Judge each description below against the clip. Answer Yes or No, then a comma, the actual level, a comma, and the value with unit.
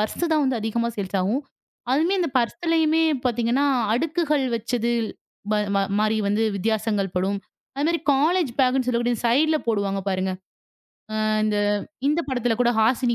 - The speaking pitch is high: Yes, high, 240 Hz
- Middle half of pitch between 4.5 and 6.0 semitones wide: Yes, average, 5.2 semitones